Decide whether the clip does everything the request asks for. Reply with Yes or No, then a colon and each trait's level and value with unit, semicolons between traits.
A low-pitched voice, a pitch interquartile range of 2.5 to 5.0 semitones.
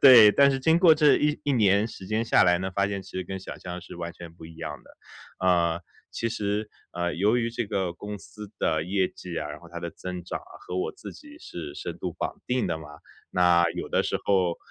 Yes: very low, 95 Hz; average, 4.4 semitones